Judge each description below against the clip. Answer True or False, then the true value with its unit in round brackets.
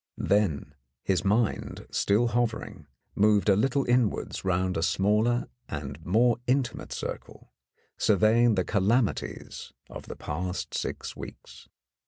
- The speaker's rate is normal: False (120 wpm)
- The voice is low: True (105 Hz)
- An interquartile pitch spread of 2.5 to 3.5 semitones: False (4.3 semitones)